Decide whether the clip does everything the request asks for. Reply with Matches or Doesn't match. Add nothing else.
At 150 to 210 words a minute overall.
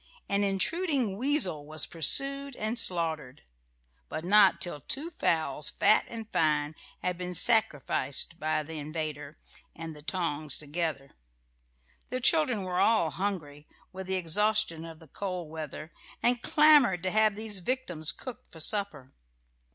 Doesn't match